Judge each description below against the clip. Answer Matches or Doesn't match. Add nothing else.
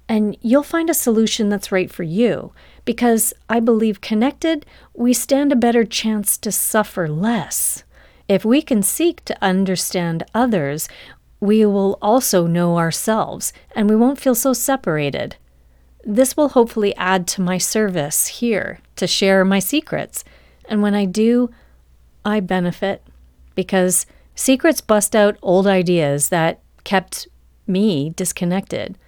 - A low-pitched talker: Doesn't match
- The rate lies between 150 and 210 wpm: Doesn't match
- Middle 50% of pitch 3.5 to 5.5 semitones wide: Matches